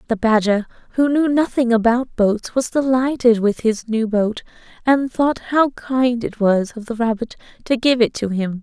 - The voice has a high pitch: Yes, high, 235 Hz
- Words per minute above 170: Yes, average, 190 wpm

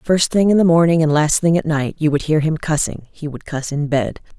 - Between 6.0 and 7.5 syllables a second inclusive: No, 5.4 syllables/s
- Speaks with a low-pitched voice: No, medium, 155 Hz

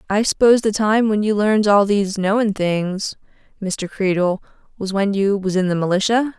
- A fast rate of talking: No, average, 190 wpm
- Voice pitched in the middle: No, high, 200 Hz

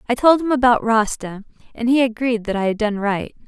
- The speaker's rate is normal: No, fast, 225 wpm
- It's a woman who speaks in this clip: Yes, female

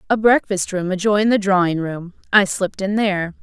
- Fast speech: No, average, 195 wpm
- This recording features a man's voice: No, female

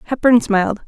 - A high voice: Yes, high, 225 Hz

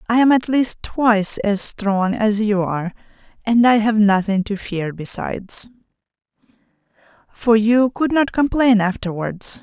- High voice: Yes, high, 215 Hz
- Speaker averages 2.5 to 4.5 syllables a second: Yes, 4.3 syllables/s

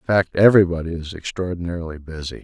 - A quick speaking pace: No, average, 150 wpm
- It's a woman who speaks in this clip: No, male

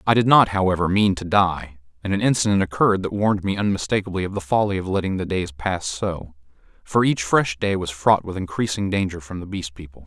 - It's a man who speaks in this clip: Yes, male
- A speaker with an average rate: No, fast, 215 wpm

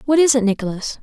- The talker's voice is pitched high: Yes, high, 245 Hz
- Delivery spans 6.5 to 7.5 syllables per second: Yes, 6.9 syllables/s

